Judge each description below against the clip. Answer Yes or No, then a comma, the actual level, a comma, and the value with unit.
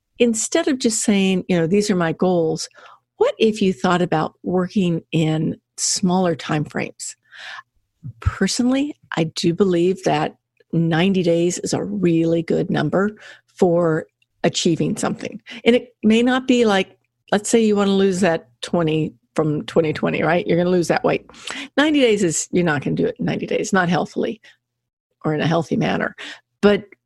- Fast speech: No, average, 170 wpm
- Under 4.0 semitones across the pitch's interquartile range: No, average, 4.5 semitones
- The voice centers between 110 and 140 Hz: No, medium, 180 Hz